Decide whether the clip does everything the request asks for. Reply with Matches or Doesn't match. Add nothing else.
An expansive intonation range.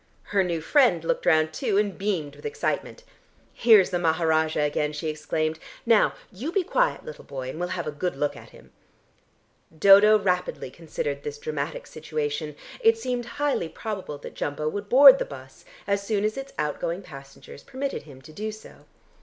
Matches